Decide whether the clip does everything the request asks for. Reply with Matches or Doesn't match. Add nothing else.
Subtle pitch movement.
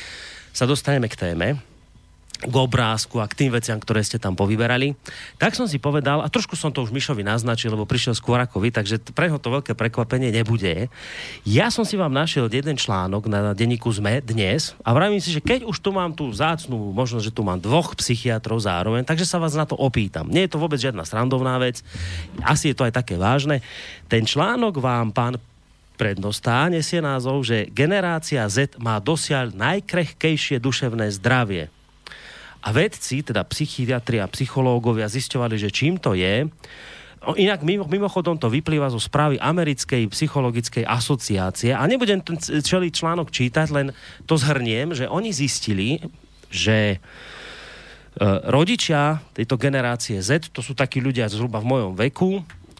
Doesn't match